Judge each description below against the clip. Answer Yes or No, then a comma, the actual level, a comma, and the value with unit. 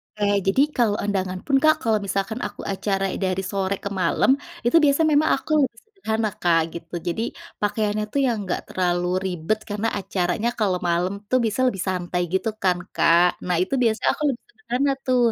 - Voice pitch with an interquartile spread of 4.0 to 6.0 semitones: Yes, average, 4.6 semitones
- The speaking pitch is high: Yes, high, 205 Hz